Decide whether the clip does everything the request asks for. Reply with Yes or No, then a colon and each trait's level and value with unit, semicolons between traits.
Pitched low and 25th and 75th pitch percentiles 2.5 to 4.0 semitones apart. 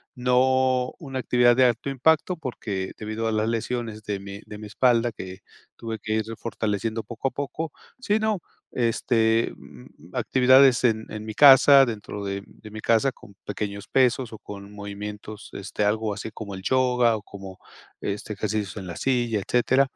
Yes: low, 110 Hz; average, 3.4 semitones